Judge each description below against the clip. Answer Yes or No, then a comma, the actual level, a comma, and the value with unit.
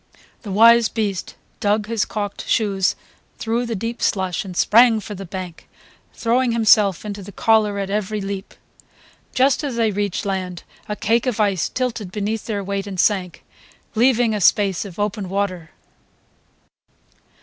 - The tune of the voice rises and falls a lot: No, narrow, 2.6 semitones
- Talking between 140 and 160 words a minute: Yes, average, 155 wpm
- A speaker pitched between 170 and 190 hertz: No, high, 205 Hz